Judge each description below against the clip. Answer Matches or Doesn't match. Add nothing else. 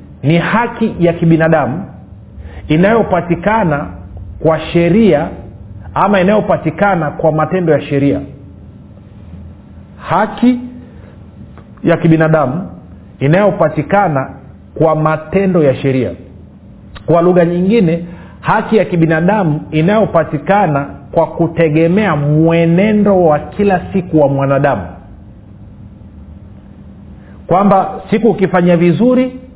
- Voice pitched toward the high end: Doesn't match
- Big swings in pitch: Matches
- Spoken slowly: Matches